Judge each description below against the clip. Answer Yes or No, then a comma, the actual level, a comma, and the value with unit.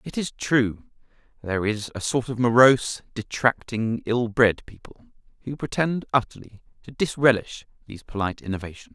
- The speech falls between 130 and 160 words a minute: Yes, average, 140 wpm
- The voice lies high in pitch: No, low, 120 Hz